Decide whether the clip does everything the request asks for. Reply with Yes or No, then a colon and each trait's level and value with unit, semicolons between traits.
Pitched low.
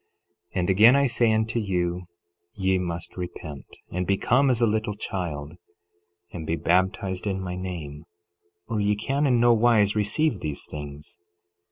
Yes: very low, 95 Hz